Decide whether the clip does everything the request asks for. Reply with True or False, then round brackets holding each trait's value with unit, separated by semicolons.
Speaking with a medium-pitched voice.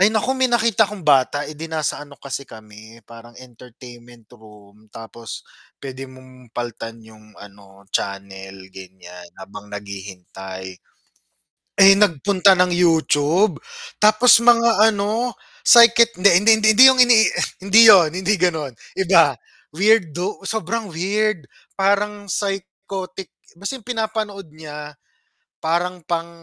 True (165 Hz)